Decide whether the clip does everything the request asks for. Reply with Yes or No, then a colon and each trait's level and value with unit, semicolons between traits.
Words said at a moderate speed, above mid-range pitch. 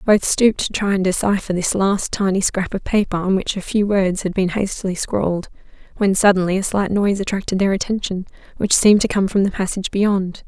No: fast, 210 wpm; high, 195 Hz